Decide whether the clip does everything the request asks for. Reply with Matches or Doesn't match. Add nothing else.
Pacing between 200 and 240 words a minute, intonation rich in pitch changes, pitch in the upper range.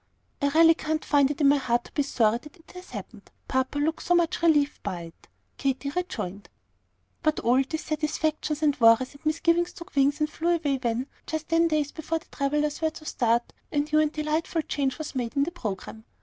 Doesn't match